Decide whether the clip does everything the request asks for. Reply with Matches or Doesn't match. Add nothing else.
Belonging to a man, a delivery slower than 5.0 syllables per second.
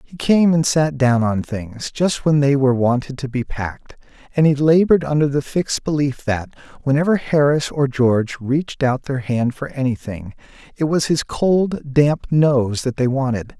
Matches